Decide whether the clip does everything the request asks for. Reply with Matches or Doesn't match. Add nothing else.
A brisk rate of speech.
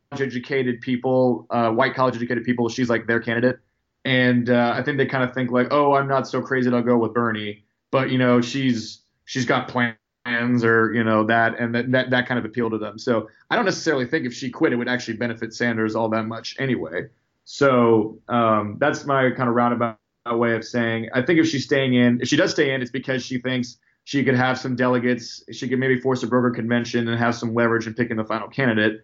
Matches